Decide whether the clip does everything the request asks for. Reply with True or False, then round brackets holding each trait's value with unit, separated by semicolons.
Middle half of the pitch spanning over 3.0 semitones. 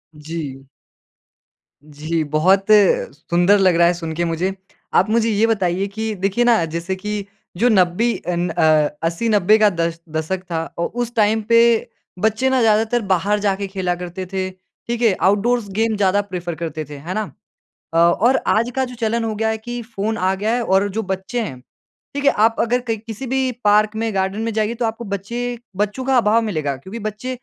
True (4.2 semitones)